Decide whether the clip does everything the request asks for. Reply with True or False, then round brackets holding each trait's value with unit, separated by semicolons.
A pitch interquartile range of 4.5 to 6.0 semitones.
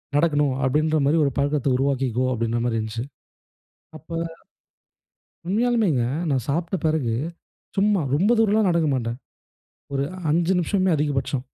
True (5.0 semitones)